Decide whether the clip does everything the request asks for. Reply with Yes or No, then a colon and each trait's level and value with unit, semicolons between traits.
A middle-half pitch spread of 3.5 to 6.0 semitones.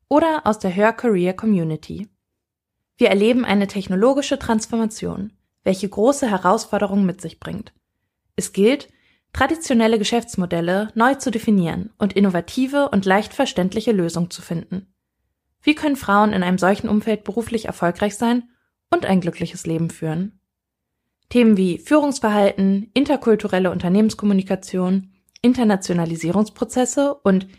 Yes: average, 3.9 semitones